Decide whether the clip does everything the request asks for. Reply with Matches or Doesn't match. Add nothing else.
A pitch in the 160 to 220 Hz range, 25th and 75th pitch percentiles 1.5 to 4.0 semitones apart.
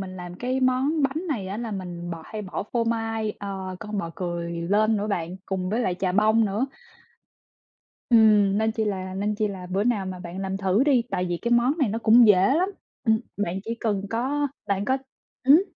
Matches